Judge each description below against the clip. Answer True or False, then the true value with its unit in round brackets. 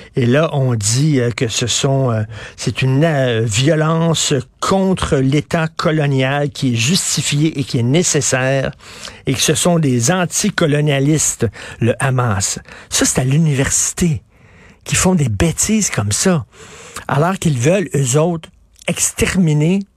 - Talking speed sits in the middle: False (130 wpm)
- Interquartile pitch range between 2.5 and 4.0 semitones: False (4.8 semitones)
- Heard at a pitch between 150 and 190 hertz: False (140 Hz)